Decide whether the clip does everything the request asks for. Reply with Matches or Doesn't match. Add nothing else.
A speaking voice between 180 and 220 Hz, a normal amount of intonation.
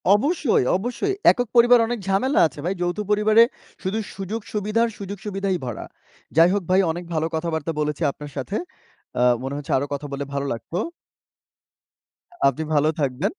Doesn't match